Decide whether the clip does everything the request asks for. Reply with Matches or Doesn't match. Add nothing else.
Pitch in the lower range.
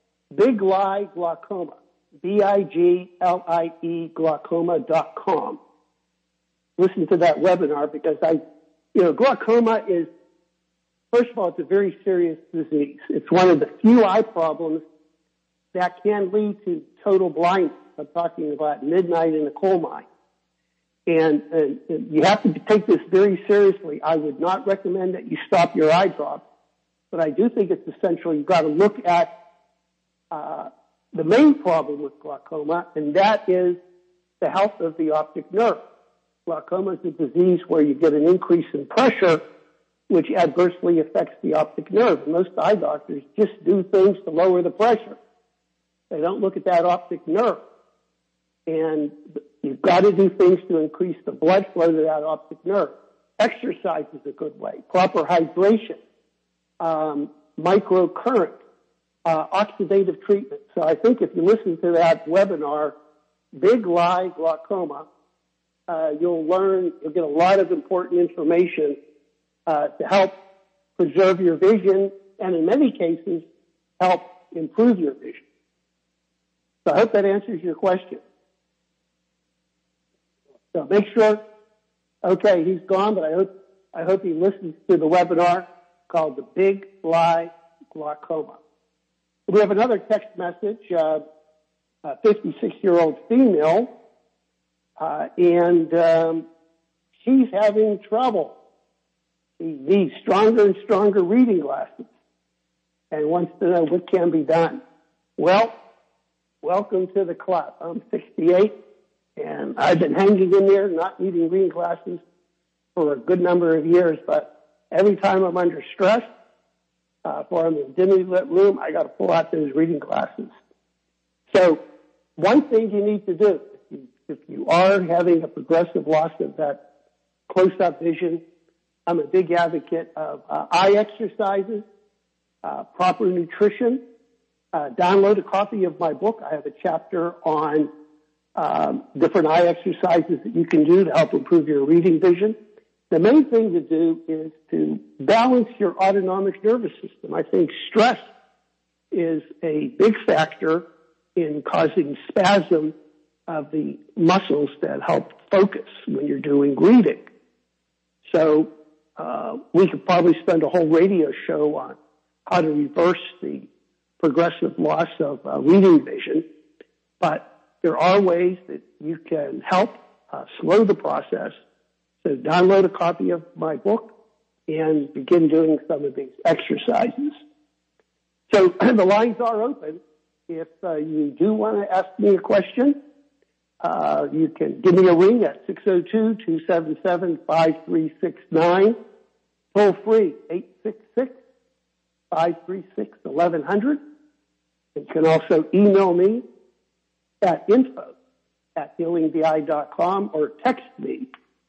Doesn't match